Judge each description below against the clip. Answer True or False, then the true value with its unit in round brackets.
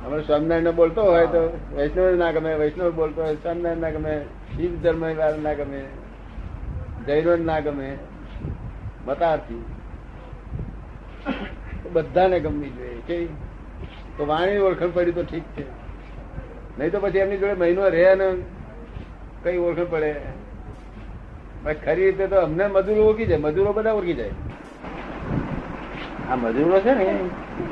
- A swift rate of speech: False (130 wpm)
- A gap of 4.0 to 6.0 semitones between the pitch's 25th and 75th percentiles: False (3.3 semitones)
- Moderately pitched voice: True (165 Hz)